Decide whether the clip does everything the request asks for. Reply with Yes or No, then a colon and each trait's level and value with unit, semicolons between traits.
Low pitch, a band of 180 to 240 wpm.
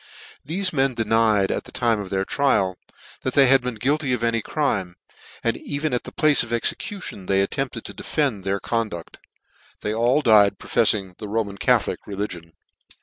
Yes: low, 115 Hz; average, 185 wpm